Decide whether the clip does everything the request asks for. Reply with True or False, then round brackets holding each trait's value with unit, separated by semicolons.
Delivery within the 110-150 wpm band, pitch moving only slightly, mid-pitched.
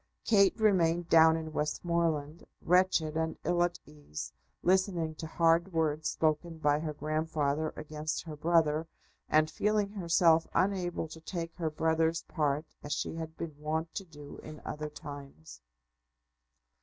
True (145 wpm; 2.0 semitones; 160 Hz)